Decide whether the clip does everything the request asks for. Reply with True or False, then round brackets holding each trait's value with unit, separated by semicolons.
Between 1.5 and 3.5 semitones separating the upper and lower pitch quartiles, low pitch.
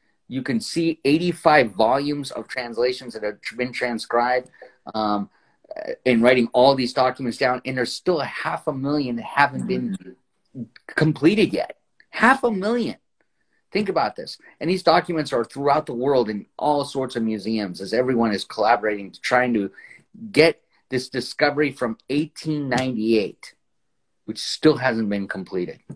False (4.3 semitones; 125 Hz)